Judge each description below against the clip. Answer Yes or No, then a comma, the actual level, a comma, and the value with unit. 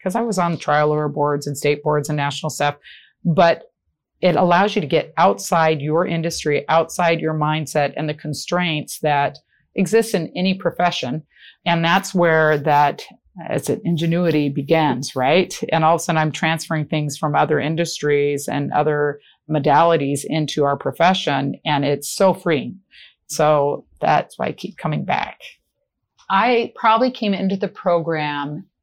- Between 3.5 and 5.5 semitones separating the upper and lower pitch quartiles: No, average, 3.0 semitones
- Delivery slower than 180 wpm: Yes, average, 160 wpm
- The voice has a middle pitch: Yes, medium, 155 Hz